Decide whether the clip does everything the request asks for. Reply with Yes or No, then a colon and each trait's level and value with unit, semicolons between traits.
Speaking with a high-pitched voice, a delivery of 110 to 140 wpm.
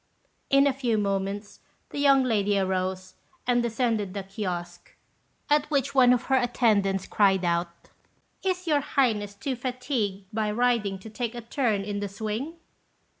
No: high, 220 Hz; average, 155 wpm